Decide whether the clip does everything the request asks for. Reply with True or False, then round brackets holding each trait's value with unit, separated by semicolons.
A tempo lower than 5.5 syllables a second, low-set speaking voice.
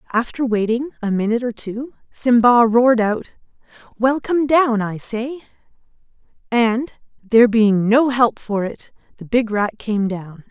False (4.3 syllables/s; 230 Hz)